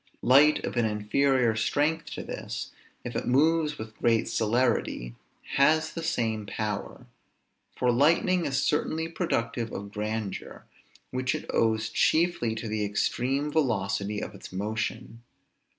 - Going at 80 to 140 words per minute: Yes, slow, 135 wpm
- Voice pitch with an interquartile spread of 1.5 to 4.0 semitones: No, wide, 5.4 semitones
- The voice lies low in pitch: Yes, low, 120 Hz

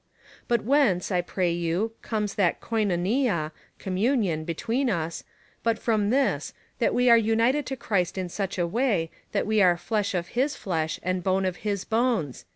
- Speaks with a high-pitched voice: Yes, high, 200 Hz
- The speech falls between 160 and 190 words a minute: Yes, average, 170 wpm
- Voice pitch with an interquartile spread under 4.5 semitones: No, average, 4.8 semitones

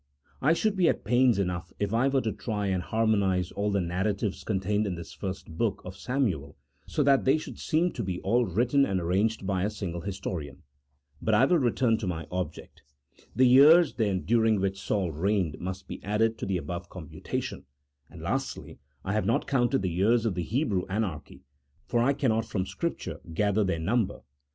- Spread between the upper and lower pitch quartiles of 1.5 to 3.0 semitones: No, average, 4.3 semitones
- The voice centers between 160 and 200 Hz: No, low, 105 Hz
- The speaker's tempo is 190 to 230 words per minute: Yes, average, 195 wpm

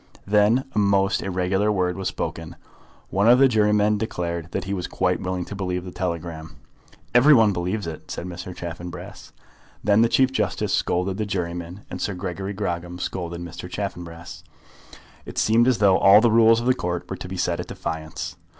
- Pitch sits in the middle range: No, very low, 95 Hz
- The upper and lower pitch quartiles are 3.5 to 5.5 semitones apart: No, average, 3.1 semitones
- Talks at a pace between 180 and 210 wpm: Yes, average, 185 wpm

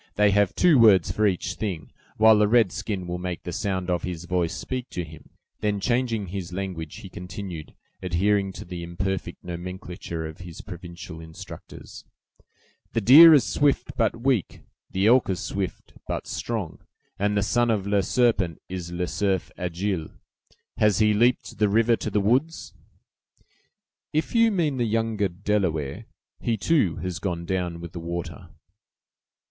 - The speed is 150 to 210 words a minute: Yes, average, 165 wpm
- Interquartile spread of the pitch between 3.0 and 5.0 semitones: Yes, average, 4.0 semitones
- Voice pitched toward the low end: Yes, very low, 95 Hz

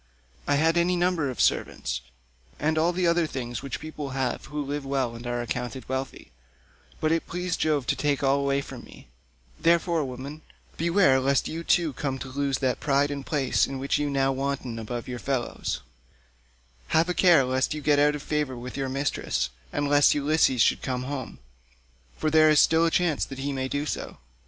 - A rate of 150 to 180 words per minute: No, average, 200 wpm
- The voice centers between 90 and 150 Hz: Yes, medium, 140 Hz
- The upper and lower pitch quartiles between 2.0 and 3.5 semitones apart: Yes, average, 3.0 semitones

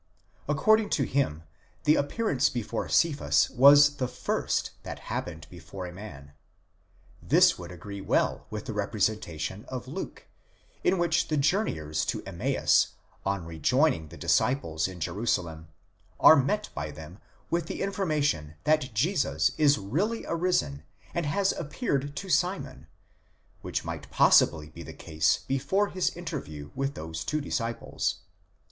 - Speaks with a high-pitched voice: No, low, 125 Hz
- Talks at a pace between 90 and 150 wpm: Yes, average, 140 wpm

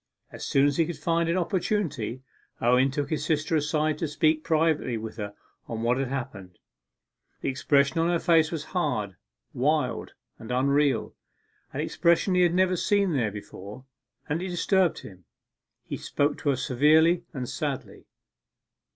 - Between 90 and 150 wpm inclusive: No, average, 160 wpm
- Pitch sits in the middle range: Yes, medium, 150 Hz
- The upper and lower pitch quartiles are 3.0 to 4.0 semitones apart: No, average, 4.8 semitones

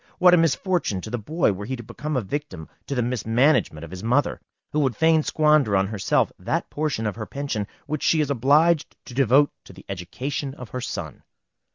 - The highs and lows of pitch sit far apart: Yes, wide, 5.7 semitones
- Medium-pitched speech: No, low, 130 Hz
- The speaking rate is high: Yes, fast, 210 wpm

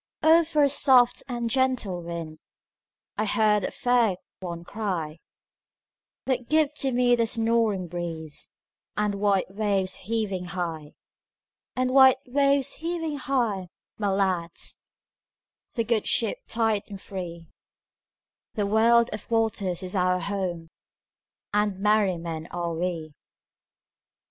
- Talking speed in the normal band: No, slow, 105 wpm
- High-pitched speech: Yes, high, 210 Hz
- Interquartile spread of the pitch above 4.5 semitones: Yes, average, 5.2 semitones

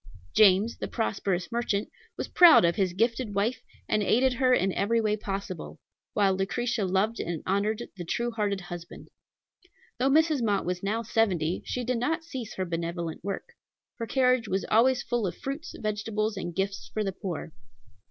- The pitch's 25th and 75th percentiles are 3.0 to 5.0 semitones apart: Yes, average, 3.9 semitones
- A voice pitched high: Yes, high, 210 Hz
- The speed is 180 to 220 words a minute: No, average, 170 wpm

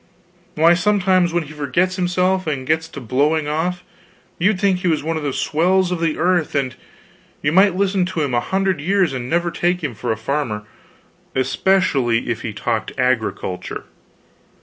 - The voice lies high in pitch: No, medium, 160 Hz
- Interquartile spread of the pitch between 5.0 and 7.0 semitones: Yes, wide, 5.4 semitones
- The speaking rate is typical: Yes, average, 175 wpm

